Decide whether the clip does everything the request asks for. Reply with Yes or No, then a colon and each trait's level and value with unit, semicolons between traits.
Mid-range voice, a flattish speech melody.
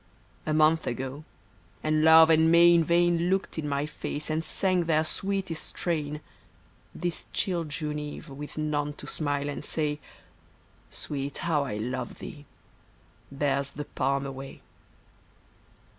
Yes: medium, 150 Hz; narrow, 2.3 semitones